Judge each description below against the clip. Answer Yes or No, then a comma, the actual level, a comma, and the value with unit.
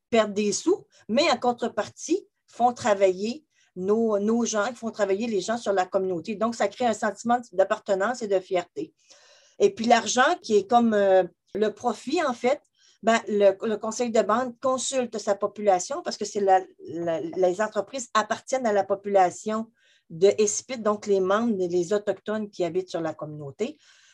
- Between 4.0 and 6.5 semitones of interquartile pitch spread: No, average, 3.5 semitones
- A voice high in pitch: Yes, high, 215 Hz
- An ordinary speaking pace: Yes, average, 170 wpm